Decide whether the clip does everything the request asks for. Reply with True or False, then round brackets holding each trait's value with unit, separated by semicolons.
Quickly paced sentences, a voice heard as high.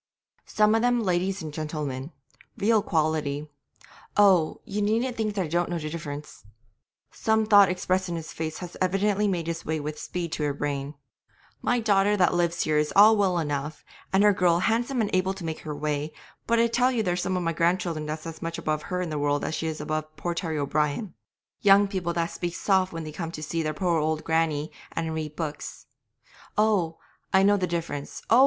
False (210 wpm; 170 Hz)